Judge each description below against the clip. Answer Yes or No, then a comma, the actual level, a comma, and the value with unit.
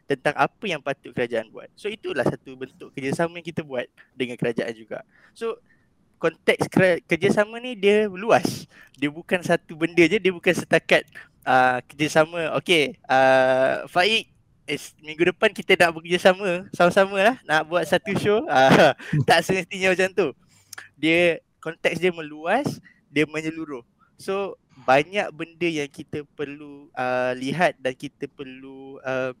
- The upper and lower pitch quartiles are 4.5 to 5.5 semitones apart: Yes, average, 5.0 semitones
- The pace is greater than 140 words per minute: Yes, average, 150 wpm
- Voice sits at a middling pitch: Yes, medium, 165 Hz